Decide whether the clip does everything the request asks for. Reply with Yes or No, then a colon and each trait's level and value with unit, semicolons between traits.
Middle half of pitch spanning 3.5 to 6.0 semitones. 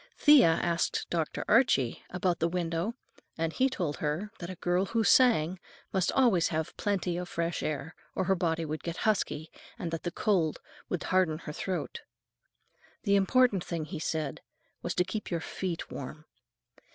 No: average, 3.1 semitones